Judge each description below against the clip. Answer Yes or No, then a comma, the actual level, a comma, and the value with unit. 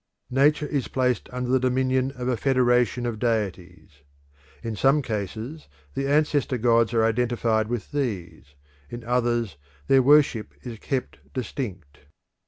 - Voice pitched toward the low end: Yes, low, 120 Hz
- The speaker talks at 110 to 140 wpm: Yes, slow, 135 wpm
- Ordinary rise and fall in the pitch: Yes, average, 3.0 semitones